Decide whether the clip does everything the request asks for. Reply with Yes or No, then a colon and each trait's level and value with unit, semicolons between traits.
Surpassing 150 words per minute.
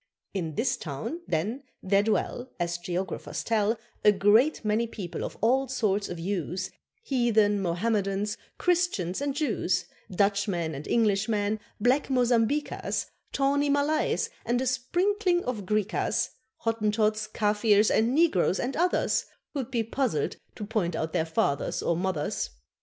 No: slow, 135 wpm